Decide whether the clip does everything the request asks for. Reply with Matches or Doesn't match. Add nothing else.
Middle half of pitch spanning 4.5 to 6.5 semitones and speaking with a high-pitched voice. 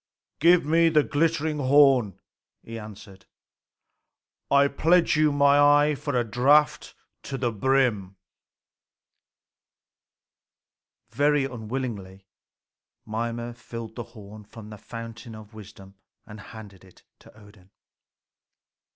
Doesn't match